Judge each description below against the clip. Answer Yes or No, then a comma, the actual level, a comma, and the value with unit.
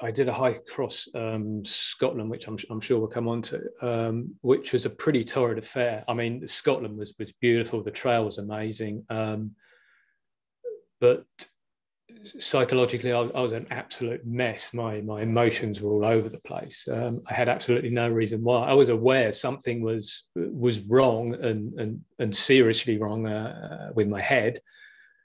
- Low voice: Yes, low, 115 Hz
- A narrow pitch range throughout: Yes, narrow, 1.9 semitones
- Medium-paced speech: Yes, average, 170 wpm